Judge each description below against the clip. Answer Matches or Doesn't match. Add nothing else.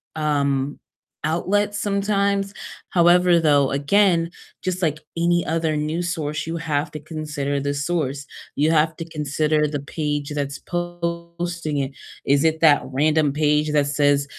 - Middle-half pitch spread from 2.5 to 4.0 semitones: Matches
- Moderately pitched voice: Matches